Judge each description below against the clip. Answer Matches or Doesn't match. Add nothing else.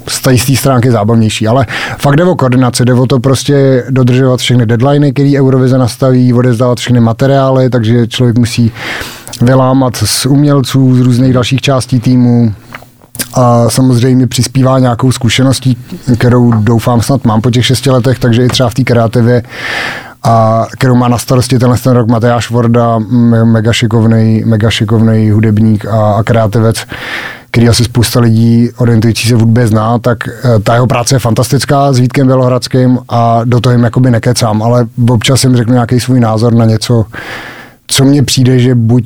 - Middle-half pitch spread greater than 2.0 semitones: Doesn't match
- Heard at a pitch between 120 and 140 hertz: Matches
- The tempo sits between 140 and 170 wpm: Matches